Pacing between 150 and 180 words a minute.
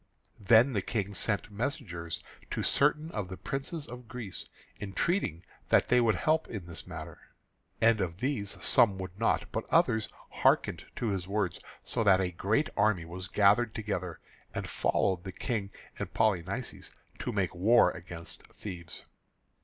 Yes: average, 155 wpm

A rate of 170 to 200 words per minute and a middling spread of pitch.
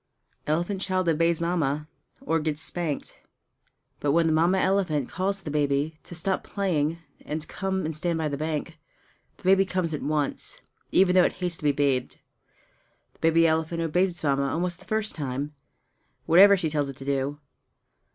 Yes: average, 180 wpm; average, 3.4 semitones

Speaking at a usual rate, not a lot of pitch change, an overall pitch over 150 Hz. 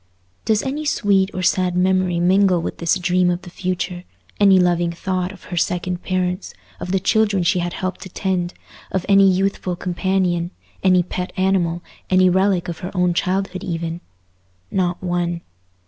Yes: average, 155 wpm; narrow, 1.4 semitones; medium, 185 Hz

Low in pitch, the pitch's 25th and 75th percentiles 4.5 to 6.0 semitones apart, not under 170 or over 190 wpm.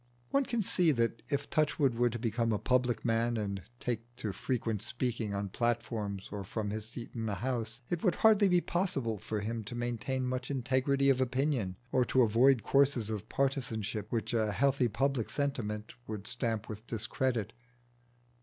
No: low, 120 Hz; average, 3.3 semitones; average, 175 wpm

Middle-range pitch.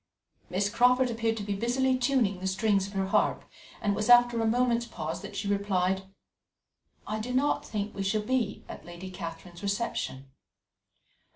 No: high, 205 Hz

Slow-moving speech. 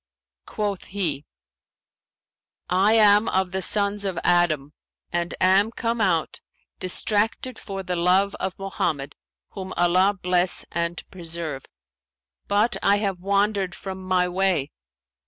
Yes: slow, 120 wpm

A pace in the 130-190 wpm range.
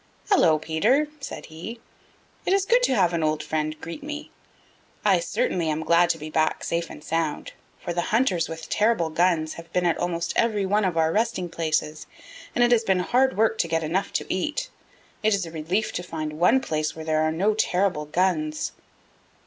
No: average, 200 wpm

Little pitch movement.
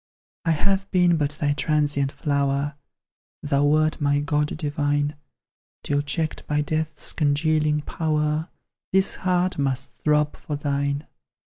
Yes: narrow, 1.5 semitones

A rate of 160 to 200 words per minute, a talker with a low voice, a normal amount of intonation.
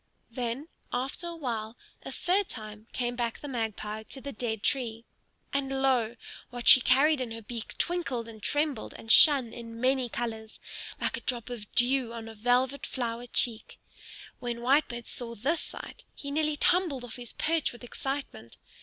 No: average, 170 wpm; high, 245 Hz; average, 3.1 semitones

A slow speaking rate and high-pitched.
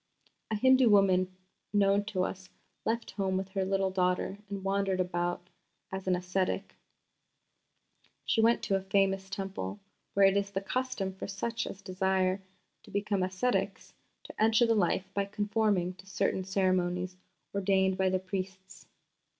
No: average, 150 wpm; high, 195 Hz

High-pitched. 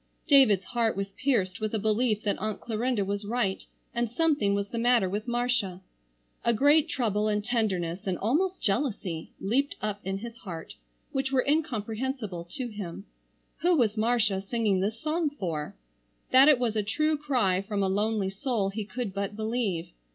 Yes: high, 220 Hz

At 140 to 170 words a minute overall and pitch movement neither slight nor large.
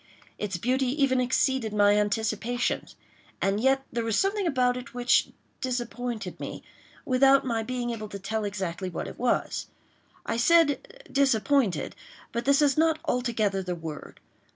Yes: average, 145 wpm; average, 4.3 semitones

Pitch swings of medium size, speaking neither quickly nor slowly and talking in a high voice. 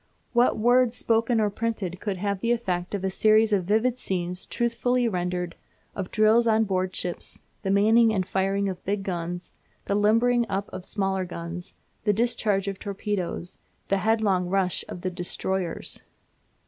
Yes: average, 3.3 semitones; average, 160 wpm; high, 200 Hz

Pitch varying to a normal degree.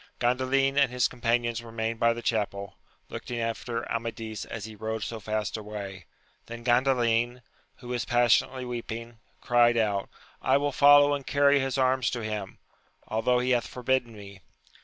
No: narrow, 2.2 semitones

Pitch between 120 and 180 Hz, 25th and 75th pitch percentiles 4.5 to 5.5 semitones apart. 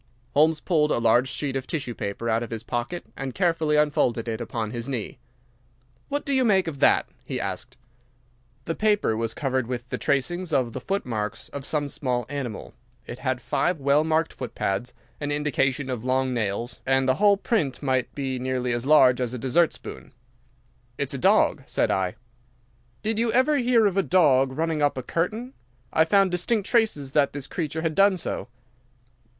Yes: medium, 140 Hz; average, 5.2 semitones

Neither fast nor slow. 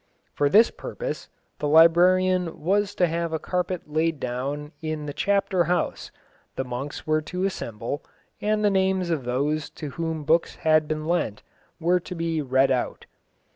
Yes: average, 165 wpm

